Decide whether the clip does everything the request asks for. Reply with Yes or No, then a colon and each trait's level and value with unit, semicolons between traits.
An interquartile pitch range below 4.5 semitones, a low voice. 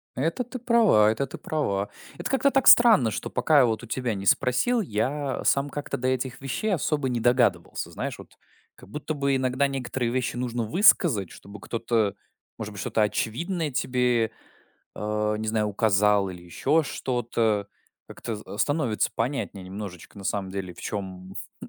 No: average, 5.1 semitones; low, 120 Hz